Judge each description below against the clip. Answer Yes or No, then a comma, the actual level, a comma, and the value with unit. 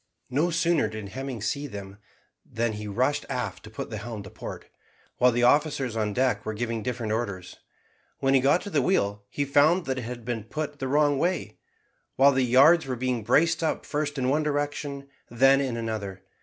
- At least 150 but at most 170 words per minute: No, average, 200 wpm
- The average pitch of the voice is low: Yes, low, 130 Hz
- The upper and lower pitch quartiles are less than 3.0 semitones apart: No, average, 4.6 semitones